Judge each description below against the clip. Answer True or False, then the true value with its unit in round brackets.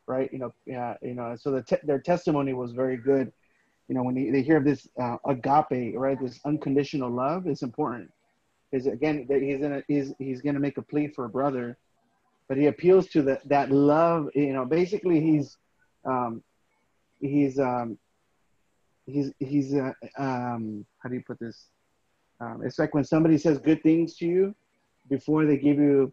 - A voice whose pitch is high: False (140 Hz)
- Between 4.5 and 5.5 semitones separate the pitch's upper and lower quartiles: False (2.5 semitones)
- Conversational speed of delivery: True (190 wpm)